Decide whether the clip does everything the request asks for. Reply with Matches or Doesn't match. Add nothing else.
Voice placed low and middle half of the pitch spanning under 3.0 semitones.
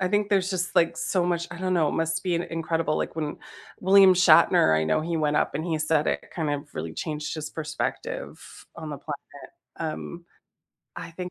Doesn't match